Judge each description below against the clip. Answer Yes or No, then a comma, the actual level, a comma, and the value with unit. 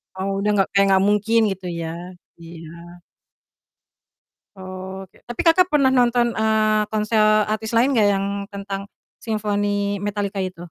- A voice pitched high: Yes, high, 205 Hz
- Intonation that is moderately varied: No, narrow, 2.2 semitones